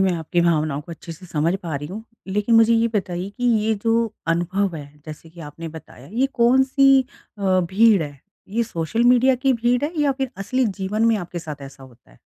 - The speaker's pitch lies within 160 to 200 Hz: Yes, high, 190 Hz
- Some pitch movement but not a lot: No, wide, 6.1 semitones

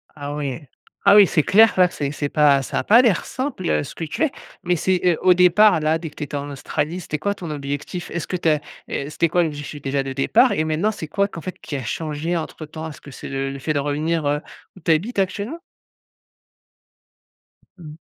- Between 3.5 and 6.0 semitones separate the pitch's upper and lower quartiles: Yes, average, 3.8 semitones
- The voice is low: No, medium, 160 Hz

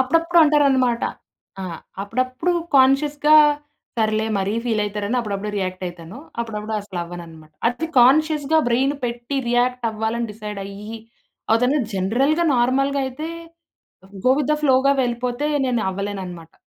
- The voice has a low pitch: No, high, 240 Hz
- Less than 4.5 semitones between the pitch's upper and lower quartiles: No, average, 5.0 semitones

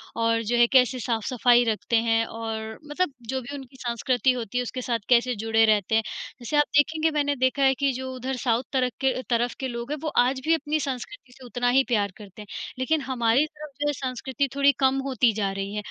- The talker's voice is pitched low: No, very high, 250 Hz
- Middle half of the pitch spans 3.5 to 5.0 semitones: No, average, 3.0 semitones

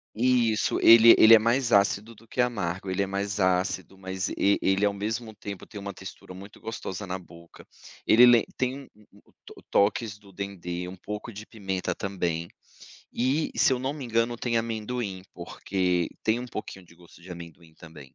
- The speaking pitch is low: Yes, low, 100 Hz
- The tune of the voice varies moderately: Yes, average, 3.7 semitones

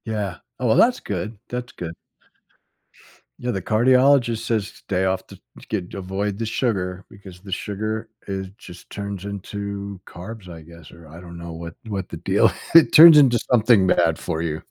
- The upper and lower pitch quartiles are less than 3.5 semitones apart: No, average, 3.8 semitones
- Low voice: Yes, low, 100 Hz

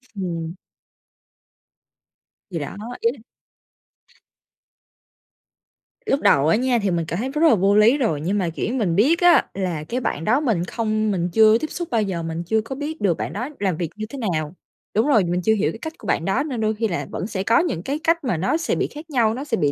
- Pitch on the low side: No, high, 215 Hz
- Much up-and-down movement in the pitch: Yes, wide, 6.7 semitones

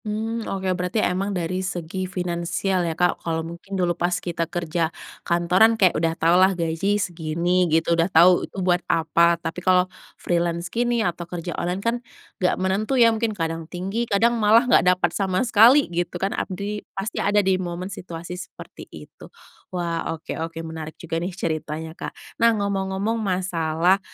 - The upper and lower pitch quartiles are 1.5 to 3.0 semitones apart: Yes, average, 2.7 semitones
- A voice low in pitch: No, medium, 180 Hz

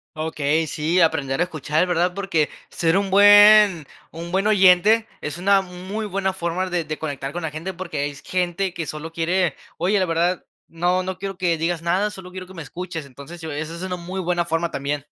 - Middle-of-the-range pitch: Yes, medium, 175 Hz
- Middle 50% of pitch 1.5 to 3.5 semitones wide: Yes, narrow, 2.6 semitones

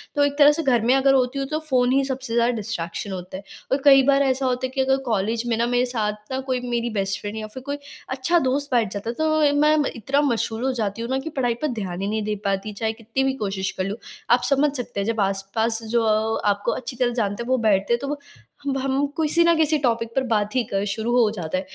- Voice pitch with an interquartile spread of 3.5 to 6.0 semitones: Yes, average, 4.1 semitones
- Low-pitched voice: No, high, 240 Hz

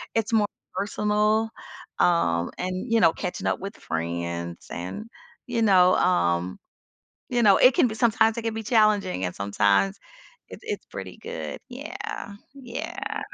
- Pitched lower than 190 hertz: No, high, 195 Hz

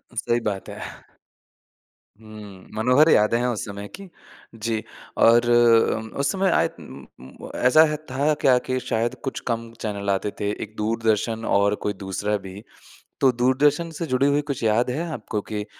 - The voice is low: Yes, low, 115 Hz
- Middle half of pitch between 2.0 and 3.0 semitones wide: No, average, 3.7 semitones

